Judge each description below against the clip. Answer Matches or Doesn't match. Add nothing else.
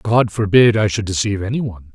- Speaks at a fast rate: Doesn't match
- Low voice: Matches